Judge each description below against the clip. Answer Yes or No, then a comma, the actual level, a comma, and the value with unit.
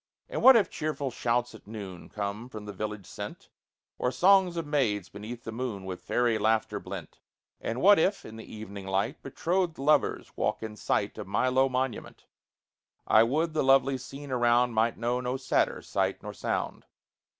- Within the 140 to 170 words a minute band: No, average, 180 wpm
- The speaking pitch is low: Yes, low, 120 Hz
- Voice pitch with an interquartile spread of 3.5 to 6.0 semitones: Yes, average, 4.1 semitones